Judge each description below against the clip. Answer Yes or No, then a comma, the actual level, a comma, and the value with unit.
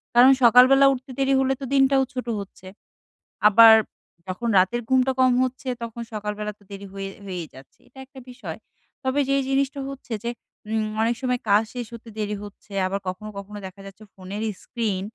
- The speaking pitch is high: Yes, high, 230 Hz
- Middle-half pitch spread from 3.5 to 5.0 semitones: Yes, average, 4.4 semitones